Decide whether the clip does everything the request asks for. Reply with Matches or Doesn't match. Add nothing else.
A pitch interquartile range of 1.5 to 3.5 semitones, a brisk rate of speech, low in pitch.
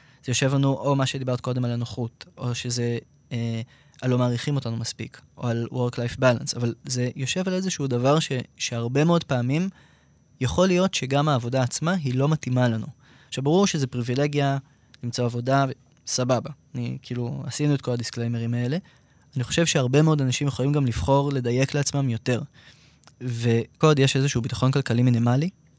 Matches